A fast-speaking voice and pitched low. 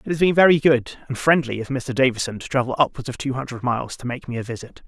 Yes: fast, 270 wpm; low, 130 Hz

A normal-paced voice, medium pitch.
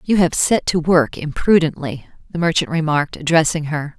Yes: average, 165 wpm; medium, 160 Hz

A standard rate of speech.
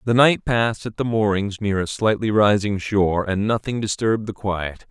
Yes: average, 195 wpm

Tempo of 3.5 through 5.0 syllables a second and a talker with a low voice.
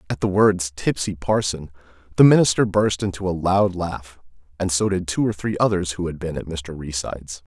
No: 5.2 syllables/s; very low, 90 Hz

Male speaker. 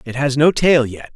Yes: male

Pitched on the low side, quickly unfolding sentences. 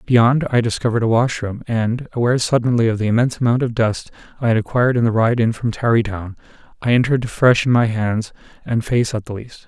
Yes: low, 115 Hz; fast, 210 wpm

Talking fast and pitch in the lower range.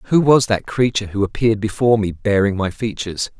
No: average, 195 wpm; low, 105 Hz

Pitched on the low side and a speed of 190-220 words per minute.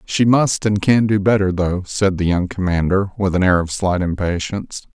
Yes: very low, 95 Hz; fast, 205 wpm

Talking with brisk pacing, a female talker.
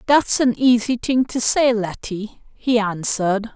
No: average, 150 wpm; female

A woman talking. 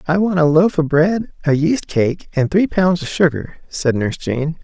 No: male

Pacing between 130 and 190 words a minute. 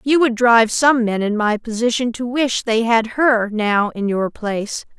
No: fast, 205 wpm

